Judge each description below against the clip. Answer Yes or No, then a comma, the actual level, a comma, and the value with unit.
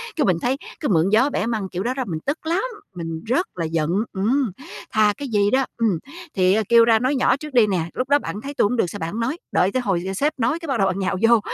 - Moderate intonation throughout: No, wide, 5.8 semitones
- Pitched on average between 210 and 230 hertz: Yes, high, 225 Hz